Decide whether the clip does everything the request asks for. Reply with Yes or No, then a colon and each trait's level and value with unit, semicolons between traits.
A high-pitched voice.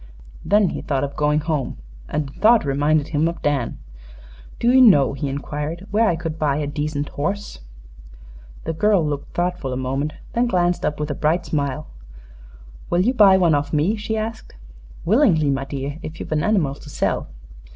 No: medium, 155 Hz